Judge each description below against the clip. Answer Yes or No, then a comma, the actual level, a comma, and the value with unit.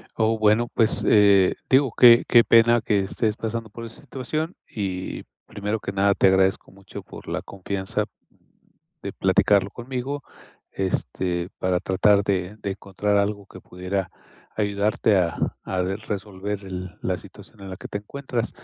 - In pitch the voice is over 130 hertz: No, low, 100 Hz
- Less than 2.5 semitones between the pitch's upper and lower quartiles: No, average, 2.8 semitones